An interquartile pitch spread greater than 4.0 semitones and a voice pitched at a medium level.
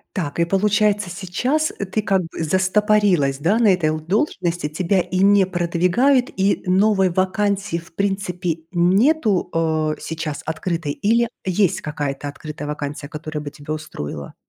Yes: average, 4.5 semitones; medium, 180 Hz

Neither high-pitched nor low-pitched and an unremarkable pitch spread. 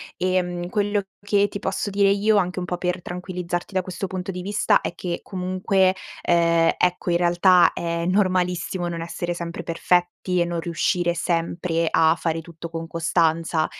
No: medium, 180 Hz; narrow, 1.7 semitones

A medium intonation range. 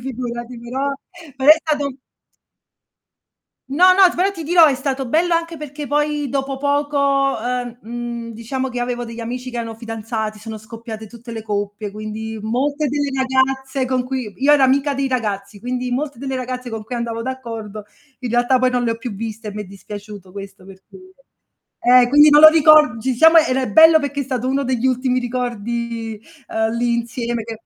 Yes: average, 3.5 semitones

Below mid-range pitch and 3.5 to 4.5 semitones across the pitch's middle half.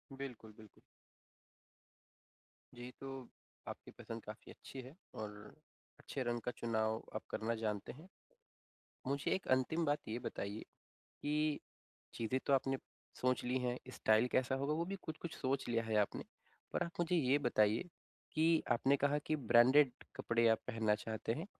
Yes: low, 125 Hz; average, 4.1 semitones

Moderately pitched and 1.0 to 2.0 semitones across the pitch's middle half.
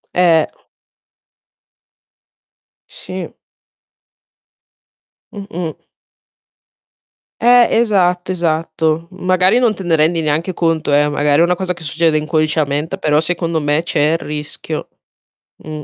No: medium, 165 Hz; average, 2.8 semitones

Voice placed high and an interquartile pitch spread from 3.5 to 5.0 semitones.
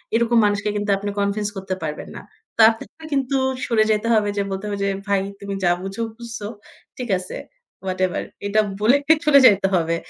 No: high, 205 Hz; average, 3.0 semitones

